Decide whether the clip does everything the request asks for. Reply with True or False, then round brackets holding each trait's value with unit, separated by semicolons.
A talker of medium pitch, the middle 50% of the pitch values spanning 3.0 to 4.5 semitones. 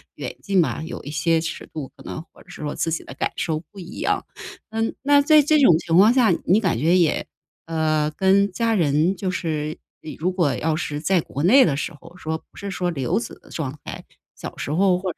True (170 Hz; 3.9 semitones)